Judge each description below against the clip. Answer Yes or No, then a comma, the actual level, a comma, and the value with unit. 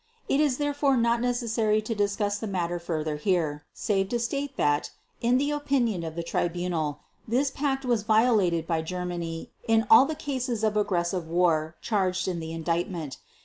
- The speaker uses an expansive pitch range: Yes, wide, 6.1 semitones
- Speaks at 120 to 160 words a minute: No, average, 170 wpm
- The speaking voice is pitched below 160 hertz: No, high, 205 Hz